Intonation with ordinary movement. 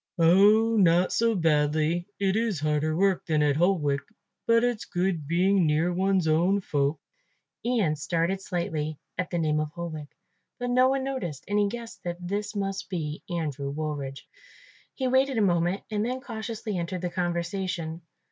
Yes: average, 4.6 semitones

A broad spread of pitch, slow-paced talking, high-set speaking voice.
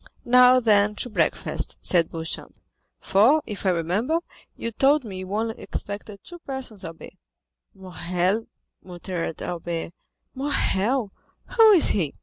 Yes: wide, 5.7 semitones; slow, 120 wpm; high, 210 Hz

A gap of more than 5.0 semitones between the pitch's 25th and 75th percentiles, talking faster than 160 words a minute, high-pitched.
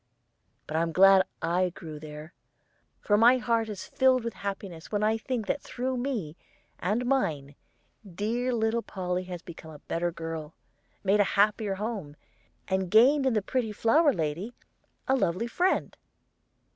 No: wide, 5.6 semitones; average, 155 wpm; high, 205 Hz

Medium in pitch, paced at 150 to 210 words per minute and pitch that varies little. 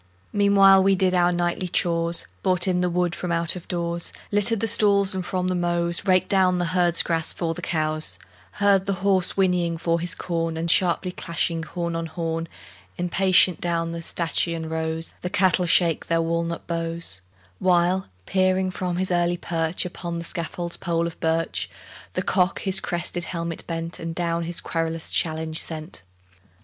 Yes: medium, 175 Hz; average, 175 wpm; narrow, 1.7 semitones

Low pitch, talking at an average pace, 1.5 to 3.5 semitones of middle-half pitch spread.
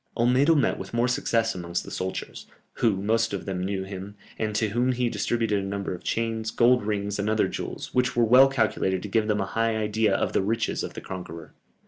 No: low, 110 Hz; fast, 220 wpm; average, 3.1 semitones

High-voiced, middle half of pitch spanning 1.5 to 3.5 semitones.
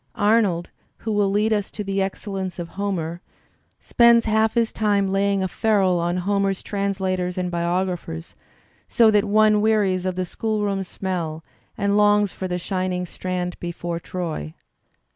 Yes: high, 195 Hz; narrow, 2.5 semitones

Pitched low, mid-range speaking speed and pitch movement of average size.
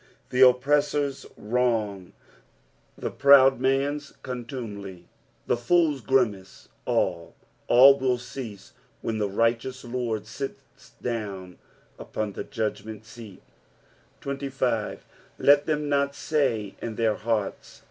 No: low, 120 Hz; slow, 115 wpm; average, 4.1 semitones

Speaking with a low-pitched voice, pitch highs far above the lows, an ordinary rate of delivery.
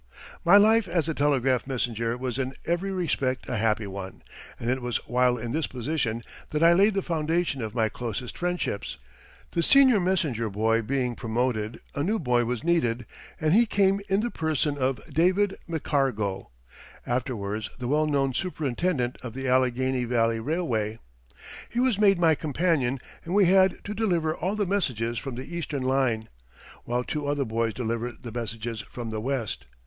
Yes: low, 130 Hz; wide, 6.5 semitones; average, 175 wpm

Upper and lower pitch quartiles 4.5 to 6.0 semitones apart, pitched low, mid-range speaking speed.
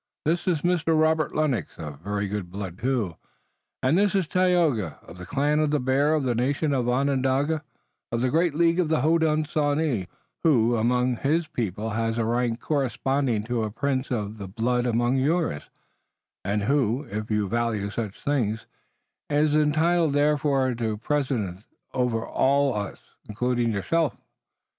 Yes: average, 5.2 semitones; low, 130 Hz; average, 160 wpm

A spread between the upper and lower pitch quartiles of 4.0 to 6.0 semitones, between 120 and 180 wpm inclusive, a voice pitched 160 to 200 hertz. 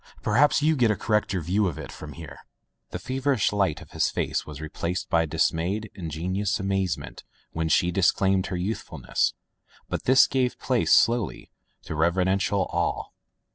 No: average, 4.3 semitones; average, 155 wpm; very low, 95 Hz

